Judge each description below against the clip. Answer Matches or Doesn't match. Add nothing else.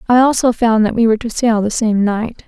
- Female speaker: Matches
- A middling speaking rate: Doesn't match